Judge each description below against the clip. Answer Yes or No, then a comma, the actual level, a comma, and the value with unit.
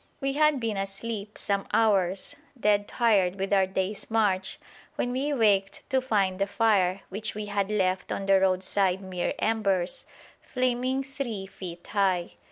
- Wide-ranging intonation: No, average, 2.9 semitones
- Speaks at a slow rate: No, average, 155 wpm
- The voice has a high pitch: Yes, high, 200 Hz